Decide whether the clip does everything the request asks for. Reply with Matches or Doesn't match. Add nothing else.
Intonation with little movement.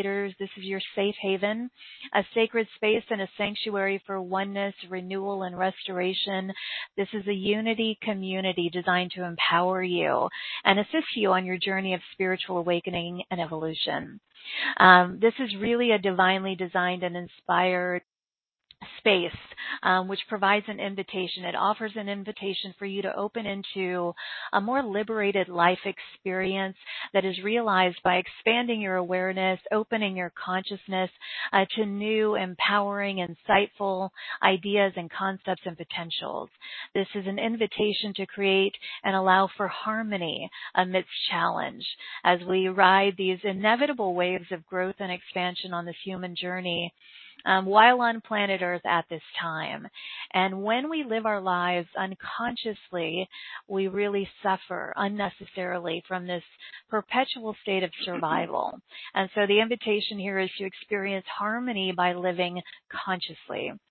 Matches